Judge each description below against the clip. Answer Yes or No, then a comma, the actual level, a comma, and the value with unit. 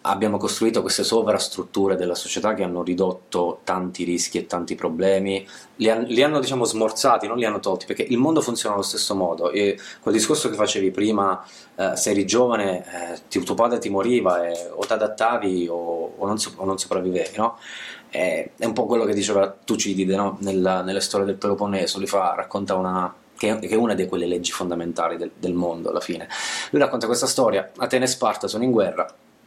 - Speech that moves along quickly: Yes, fast, 195 wpm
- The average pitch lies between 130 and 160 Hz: No, very low, 95 Hz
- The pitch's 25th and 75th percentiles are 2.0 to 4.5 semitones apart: Yes, average, 3.0 semitones